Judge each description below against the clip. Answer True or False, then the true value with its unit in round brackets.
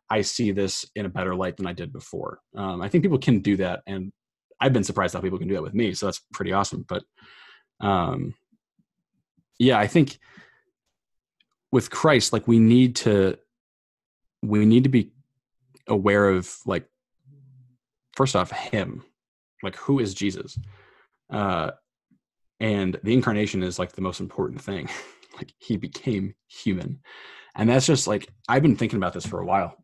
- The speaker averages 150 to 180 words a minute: True (170 wpm)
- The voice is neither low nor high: False (110 Hz)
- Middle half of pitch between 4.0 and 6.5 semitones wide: True (4.7 semitones)